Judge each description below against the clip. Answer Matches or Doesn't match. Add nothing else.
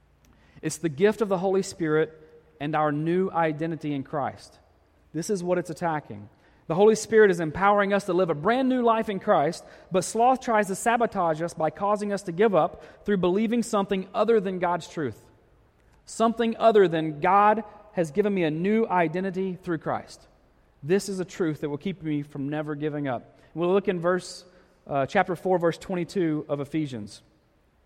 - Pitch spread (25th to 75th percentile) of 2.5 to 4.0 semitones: Doesn't match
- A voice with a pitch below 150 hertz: Doesn't match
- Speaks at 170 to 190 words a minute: Matches